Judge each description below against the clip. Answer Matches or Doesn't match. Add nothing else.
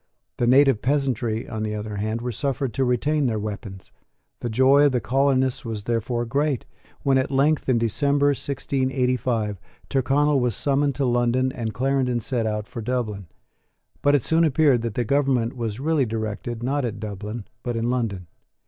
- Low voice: Matches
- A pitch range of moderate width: Matches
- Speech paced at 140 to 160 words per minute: Doesn't match